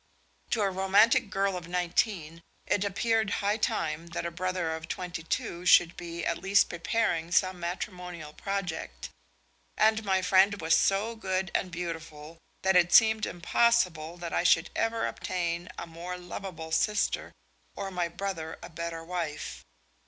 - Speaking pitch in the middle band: Yes, medium, 180 Hz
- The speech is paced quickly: No, average, 150 wpm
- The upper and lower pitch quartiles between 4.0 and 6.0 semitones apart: No, average, 2.8 semitones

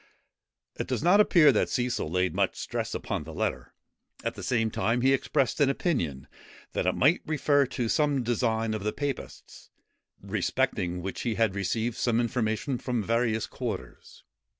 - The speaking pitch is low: Yes, low, 120 Hz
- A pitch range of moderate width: Yes, average, 4.0 semitones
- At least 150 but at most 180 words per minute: Yes, average, 165 wpm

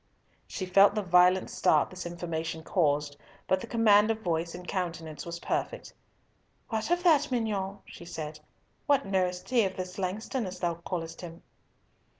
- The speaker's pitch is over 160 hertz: Yes, medium, 185 Hz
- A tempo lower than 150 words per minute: No, average, 160 wpm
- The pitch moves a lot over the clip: No, average, 3.8 semitones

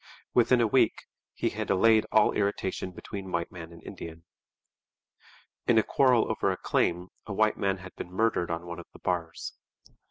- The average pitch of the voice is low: Yes, very low, 95 Hz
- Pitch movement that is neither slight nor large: Yes, average, 4.0 semitones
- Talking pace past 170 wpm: Yes, average, 180 wpm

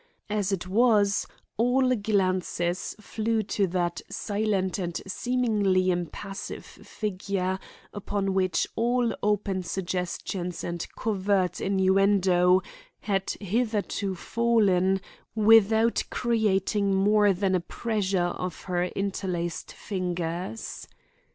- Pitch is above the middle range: Yes, high, 195 Hz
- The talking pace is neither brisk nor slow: No, slow, 95 wpm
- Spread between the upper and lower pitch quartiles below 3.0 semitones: Yes, narrow, 2.5 semitones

